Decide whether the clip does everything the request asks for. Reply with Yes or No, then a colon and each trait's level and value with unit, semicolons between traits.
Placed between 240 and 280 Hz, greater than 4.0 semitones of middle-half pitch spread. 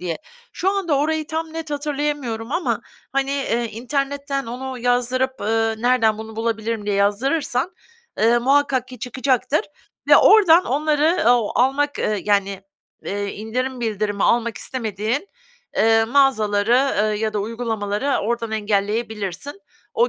Yes: high, 245 Hz; average, 4.4 semitones